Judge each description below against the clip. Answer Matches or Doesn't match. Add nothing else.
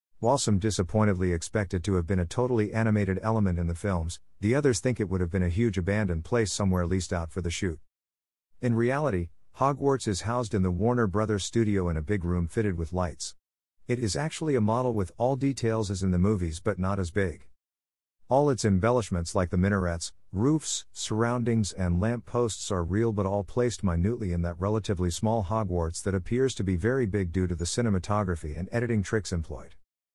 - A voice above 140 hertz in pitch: Doesn't match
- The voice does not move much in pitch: Doesn't match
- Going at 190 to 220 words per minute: Matches